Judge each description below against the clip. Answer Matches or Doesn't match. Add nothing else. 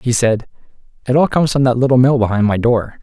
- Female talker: Doesn't match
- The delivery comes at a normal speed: Doesn't match